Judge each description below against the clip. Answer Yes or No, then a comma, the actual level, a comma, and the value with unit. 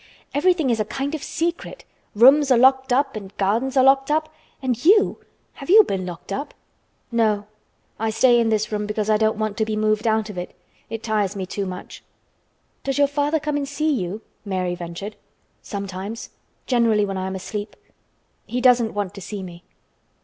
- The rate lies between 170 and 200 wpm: Yes, average, 185 wpm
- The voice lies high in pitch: Yes, high, 220 Hz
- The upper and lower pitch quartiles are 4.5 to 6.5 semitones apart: Yes, average, 5.0 semitones